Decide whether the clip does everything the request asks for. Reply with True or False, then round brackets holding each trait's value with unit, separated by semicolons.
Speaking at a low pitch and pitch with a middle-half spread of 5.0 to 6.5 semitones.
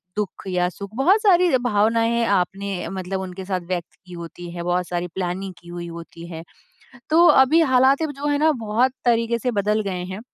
False (200 Hz; 5.6 semitones)